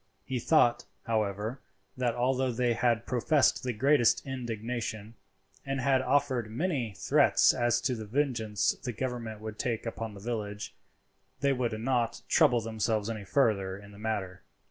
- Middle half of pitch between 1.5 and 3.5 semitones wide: Yes, average, 2.8 semitones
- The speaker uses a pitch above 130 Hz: No, low, 115 Hz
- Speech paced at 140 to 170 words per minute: Yes, average, 150 wpm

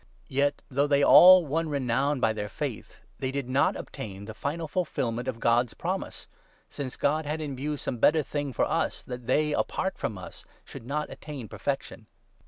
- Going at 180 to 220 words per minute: Yes, average, 190 wpm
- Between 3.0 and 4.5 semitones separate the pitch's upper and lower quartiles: Yes, average, 3.6 semitones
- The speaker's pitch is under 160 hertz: Yes, medium, 140 Hz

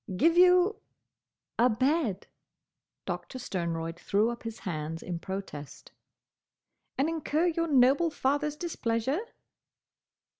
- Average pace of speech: No, slow, 105 wpm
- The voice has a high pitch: Yes, very high, 255 Hz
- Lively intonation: Yes, wide, 8.8 semitones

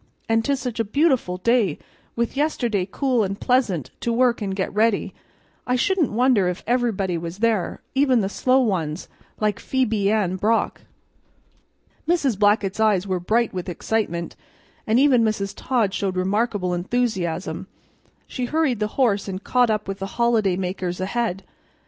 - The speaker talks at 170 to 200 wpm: No, average, 155 wpm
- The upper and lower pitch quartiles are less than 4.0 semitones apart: No, average, 4.3 semitones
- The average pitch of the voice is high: Yes, high, 215 Hz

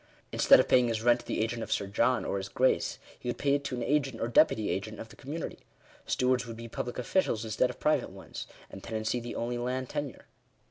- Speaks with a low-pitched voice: Yes, low, 120 Hz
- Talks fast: Yes, fast, 235 wpm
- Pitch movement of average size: No, narrow, 2.3 semitones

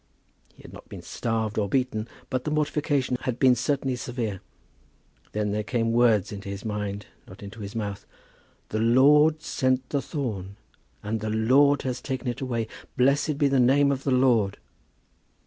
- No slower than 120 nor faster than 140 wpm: No, average, 170 wpm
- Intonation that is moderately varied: Yes, average, 4.1 semitones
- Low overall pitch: Yes, low, 125 Hz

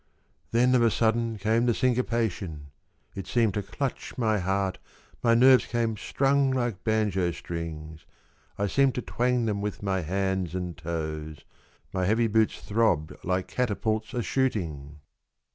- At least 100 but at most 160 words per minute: Yes, average, 150 wpm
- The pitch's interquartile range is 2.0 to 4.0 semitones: No, average, 4.7 semitones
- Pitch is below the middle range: Yes, low, 105 Hz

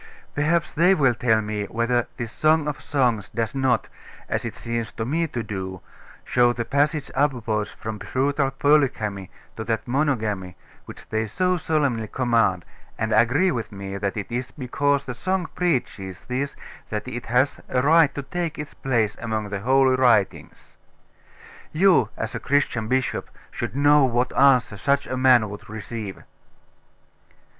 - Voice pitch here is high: No, low, 125 Hz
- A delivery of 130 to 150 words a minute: No, average, 160 wpm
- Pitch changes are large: No, average, 4.4 semitones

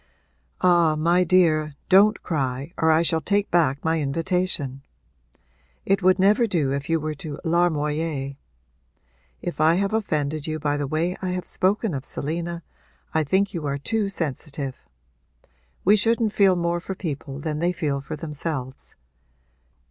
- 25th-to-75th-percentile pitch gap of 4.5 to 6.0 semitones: No, average, 3.9 semitones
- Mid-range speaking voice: Yes, medium, 165 Hz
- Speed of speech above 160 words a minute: No, average, 155 wpm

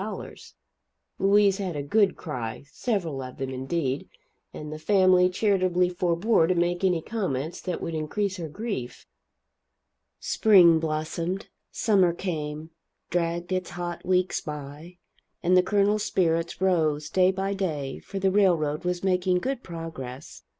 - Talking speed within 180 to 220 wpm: No, slow, 135 wpm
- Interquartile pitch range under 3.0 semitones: No, average, 3.5 semitones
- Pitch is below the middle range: No, medium, 175 Hz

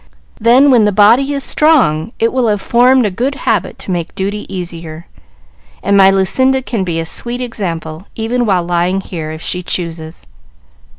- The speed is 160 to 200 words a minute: Yes, average, 175 wpm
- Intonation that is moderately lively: No, wide, 5.9 semitones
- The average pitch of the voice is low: No, high, 200 Hz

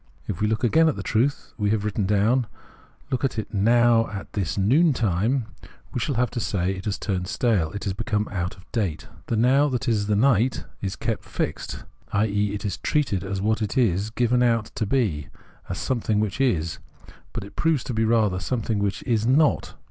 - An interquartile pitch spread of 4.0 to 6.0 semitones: No, average, 3.6 semitones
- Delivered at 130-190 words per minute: No, fast, 205 wpm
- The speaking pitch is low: Yes, low, 110 Hz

